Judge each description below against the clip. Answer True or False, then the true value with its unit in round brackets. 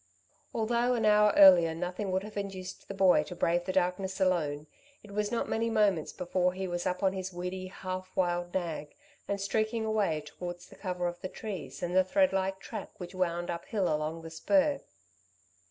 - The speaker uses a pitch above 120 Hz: True (185 Hz)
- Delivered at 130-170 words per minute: False (185 wpm)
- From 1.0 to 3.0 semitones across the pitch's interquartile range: True (2.5 semitones)